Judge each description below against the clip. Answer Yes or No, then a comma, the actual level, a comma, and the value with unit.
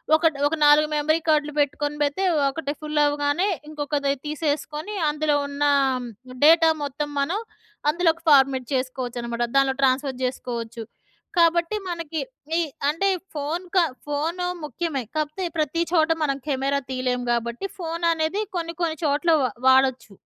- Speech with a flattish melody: No, average, 3.2 semitones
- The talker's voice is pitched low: No, very high, 295 Hz